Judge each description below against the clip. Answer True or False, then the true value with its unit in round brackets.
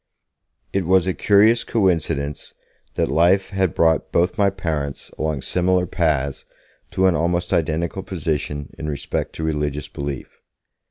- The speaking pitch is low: True (85 Hz)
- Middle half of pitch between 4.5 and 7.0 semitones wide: False (4.1 semitones)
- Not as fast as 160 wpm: True (140 wpm)